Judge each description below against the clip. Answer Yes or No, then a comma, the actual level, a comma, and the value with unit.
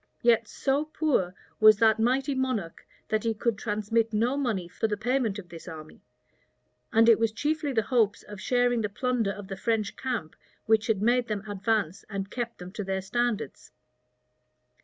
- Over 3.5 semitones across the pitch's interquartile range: No, average, 3.2 semitones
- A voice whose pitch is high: Yes, high, 220 Hz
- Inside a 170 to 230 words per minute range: Yes, average, 180 wpm